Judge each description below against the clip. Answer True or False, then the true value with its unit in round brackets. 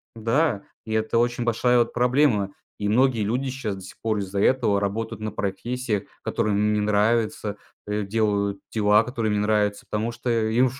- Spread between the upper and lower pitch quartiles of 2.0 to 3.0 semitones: True (2.6 semitones)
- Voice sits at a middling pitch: False (110 Hz)